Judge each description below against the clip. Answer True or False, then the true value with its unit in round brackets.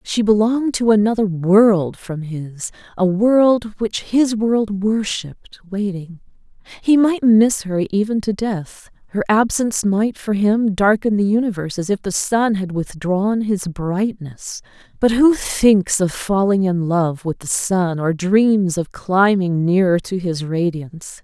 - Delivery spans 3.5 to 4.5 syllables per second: True (3.9 syllables/s)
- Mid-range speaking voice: False (200 Hz)